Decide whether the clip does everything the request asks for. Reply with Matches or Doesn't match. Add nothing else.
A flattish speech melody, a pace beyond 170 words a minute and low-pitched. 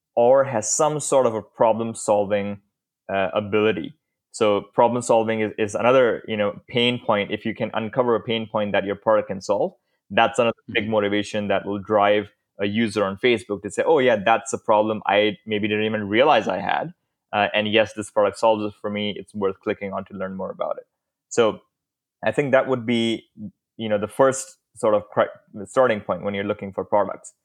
Matches